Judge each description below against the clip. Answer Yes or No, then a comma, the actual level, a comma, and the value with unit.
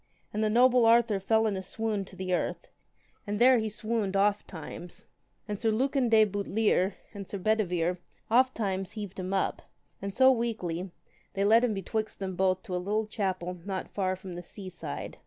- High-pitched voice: Yes, high, 205 Hz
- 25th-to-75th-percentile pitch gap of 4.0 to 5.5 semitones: No, average, 3.0 semitones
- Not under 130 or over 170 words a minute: No, average, 195 wpm